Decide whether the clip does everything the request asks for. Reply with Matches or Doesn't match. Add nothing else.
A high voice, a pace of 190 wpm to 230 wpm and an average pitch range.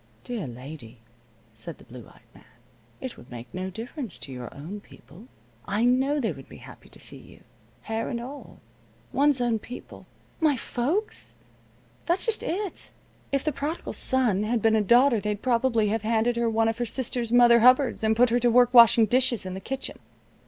Matches